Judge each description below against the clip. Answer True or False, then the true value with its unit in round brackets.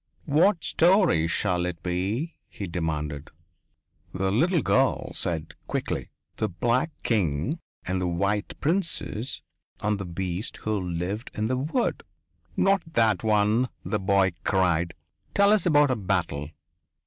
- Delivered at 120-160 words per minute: True (135 wpm)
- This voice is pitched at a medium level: False (105 Hz)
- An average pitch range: False (7.8 semitones)